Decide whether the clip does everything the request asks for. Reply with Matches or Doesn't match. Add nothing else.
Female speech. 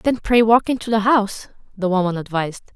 Matches